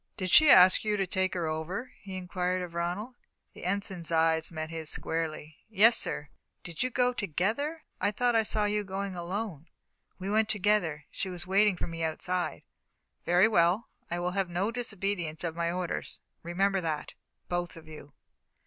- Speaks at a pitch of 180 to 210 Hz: Yes, medium, 185 Hz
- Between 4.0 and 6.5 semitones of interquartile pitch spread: No, average, 3.5 semitones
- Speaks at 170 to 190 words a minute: Yes, average, 175 wpm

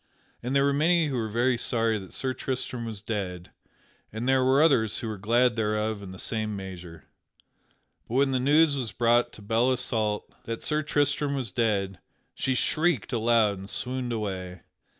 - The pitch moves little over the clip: No, average, 3.8 semitones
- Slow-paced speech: No, average, 180 wpm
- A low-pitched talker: Yes, low, 115 Hz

